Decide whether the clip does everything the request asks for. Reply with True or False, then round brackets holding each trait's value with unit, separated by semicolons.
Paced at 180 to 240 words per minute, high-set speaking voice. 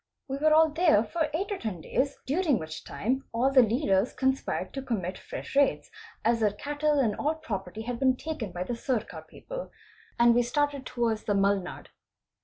True (190 wpm; 255 Hz)